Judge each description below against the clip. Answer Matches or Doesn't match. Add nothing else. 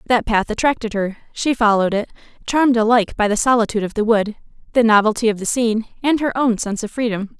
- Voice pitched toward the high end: Matches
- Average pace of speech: Doesn't match